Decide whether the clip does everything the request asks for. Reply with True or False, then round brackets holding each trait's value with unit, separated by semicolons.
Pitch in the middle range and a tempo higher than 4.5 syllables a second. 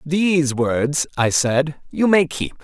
False (150 Hz; 3.5 syllables/s)